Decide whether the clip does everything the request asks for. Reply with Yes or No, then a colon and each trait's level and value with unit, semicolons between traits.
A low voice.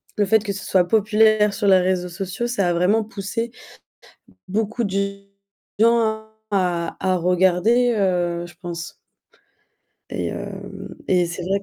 No: high, 195 Hz